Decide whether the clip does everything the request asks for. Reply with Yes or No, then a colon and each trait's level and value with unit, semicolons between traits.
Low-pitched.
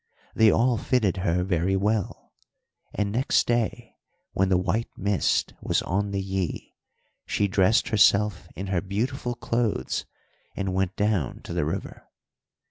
Yes: low, 100 Hz